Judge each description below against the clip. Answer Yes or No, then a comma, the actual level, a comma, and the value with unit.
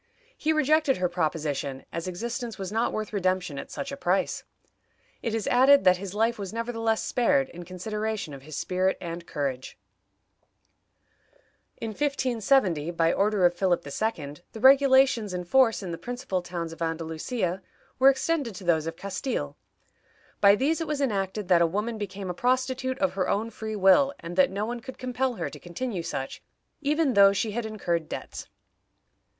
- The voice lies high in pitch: Yes, high, 205 Hz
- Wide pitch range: Yes, wide, 6.1 semitones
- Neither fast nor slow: Yes, average, 175 wpm